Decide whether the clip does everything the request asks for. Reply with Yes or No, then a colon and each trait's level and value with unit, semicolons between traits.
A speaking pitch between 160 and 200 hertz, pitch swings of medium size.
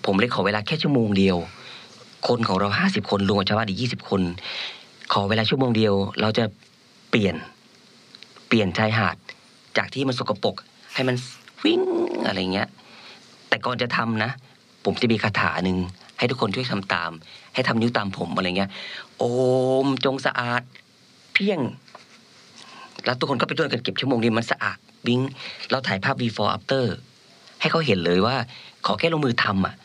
No: low, 115 Hz; average, 4.6 semitones